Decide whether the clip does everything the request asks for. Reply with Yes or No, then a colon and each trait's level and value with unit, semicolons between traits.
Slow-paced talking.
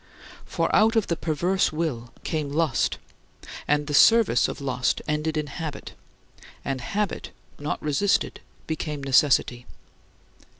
Yes: slow, 125 wpm